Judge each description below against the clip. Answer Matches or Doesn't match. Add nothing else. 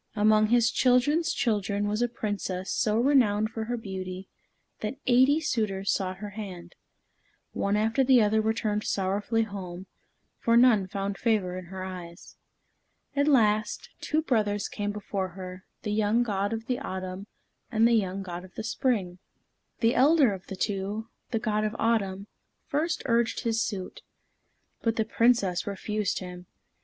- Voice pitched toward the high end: Matches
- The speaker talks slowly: Doesn't match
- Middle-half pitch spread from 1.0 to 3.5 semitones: Matches